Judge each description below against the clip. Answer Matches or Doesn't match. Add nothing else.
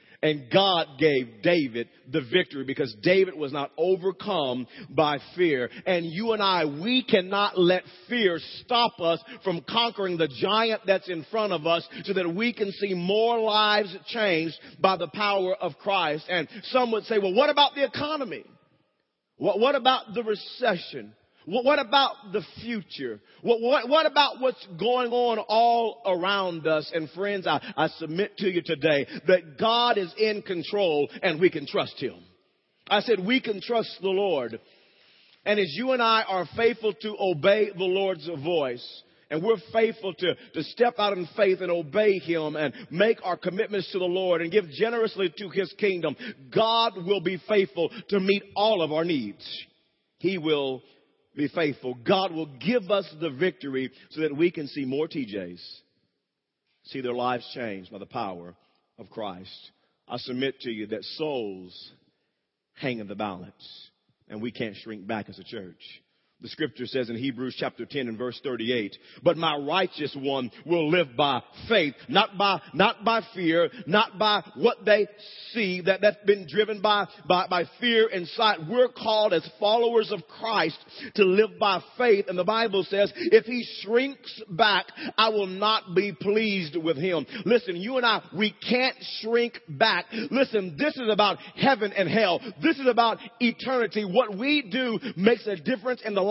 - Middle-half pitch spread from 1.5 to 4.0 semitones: Doesn't match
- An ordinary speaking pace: Matches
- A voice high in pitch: Matches